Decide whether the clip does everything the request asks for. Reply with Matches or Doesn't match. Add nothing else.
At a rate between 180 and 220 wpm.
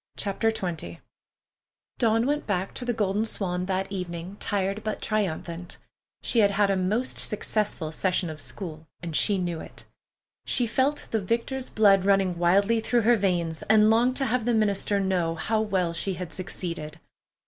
Doesn't match